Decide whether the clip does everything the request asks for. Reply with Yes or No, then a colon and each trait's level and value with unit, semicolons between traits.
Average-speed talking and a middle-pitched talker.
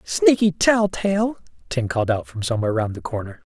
Yes: average, 190 wpm; medium, 145 Hz